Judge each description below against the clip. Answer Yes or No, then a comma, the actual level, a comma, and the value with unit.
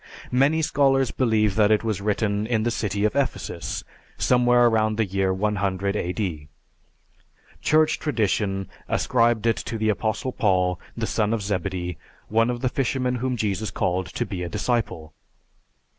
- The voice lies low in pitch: Yes, low, 110 Hz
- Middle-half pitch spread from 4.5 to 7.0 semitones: No, average, 3.8 semitones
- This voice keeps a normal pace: Yes, average, 155 wpm